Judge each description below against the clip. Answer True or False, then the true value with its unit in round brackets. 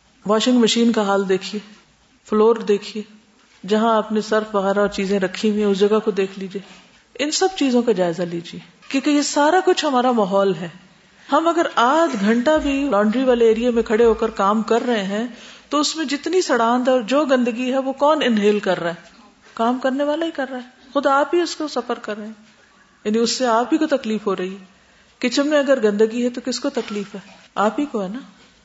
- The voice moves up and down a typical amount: True (4.4 semitones)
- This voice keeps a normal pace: False (220 wpm)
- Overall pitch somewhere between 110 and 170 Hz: False (230 Hz)